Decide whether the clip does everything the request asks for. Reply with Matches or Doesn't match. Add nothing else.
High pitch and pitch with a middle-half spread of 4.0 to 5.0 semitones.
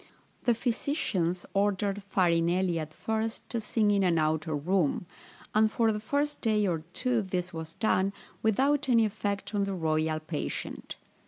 Matches